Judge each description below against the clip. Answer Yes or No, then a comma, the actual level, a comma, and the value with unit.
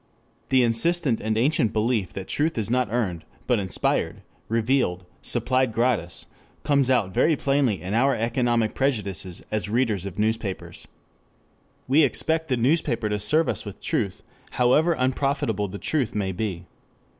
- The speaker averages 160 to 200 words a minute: No, average, 150 wpm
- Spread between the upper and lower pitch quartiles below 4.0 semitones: No, average, 4.4 semitones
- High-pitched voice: No, low, 115 Hz